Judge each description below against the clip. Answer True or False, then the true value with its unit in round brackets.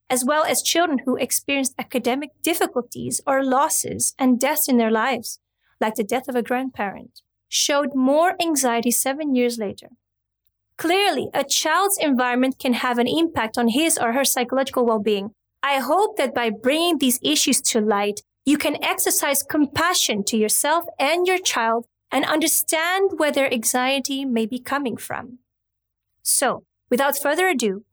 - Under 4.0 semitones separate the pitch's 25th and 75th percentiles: False (4.5 semitones)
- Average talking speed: True (155 wpm)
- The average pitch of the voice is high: True (260 Hz)